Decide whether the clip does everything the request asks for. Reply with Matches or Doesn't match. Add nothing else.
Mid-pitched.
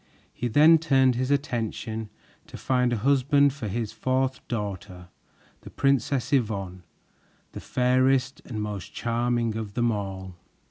Doesn't match